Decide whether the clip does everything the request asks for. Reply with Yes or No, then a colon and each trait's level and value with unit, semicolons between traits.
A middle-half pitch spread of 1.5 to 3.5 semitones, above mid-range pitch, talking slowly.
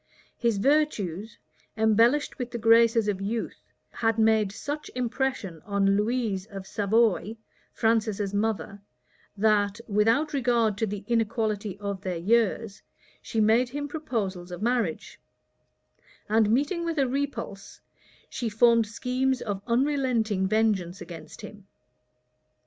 Yes: average, 3.2 semitones; high, 220 Hz; slow, 120 wpm